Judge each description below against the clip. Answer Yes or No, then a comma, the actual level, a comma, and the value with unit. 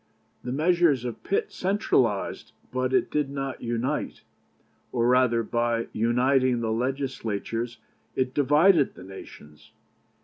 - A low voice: Yes, low, 125 Hz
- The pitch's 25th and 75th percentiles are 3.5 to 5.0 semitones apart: No, average, 2.9 semitones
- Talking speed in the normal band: No, slow, 115 wpm